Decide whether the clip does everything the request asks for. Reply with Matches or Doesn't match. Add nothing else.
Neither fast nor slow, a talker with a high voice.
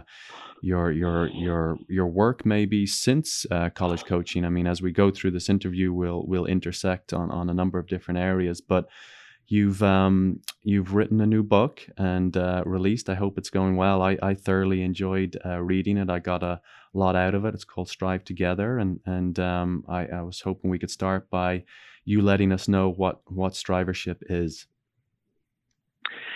Doesn't match